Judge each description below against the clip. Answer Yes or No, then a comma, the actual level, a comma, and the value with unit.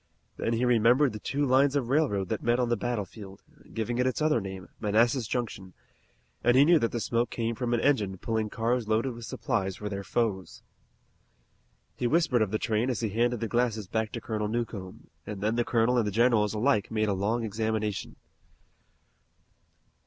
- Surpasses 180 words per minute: Yes, average, 190 wpm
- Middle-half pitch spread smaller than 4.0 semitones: Yes, narrow, 2.4 semitones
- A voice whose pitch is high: No, low, 115 Hz